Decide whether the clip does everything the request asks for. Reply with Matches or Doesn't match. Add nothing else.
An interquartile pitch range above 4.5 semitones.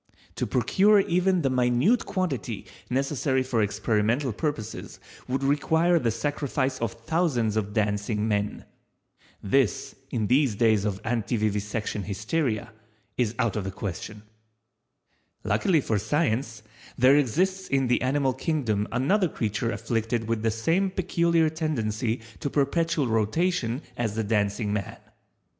Matches